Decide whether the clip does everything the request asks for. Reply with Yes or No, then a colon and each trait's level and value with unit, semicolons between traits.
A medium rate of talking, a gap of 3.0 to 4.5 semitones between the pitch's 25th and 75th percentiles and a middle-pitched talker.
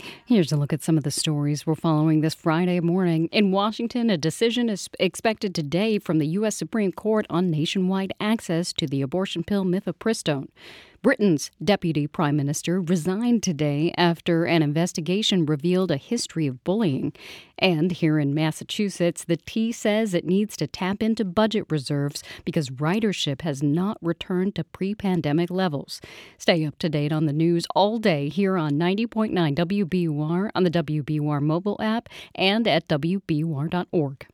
Yes: average, 160 wpm; average, 4.1 semitones; medium, 175 Hz